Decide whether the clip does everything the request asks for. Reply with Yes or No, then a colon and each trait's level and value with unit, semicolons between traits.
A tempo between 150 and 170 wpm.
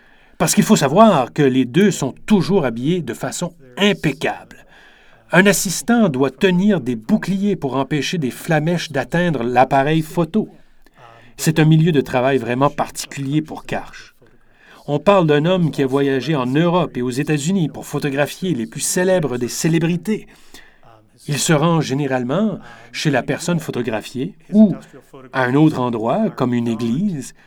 Yes: average, 155 wpm